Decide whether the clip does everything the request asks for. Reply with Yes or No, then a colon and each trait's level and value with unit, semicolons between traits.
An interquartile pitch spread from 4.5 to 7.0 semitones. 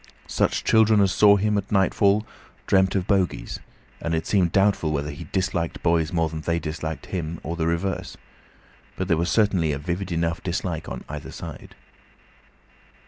No: average, 3.2 semitones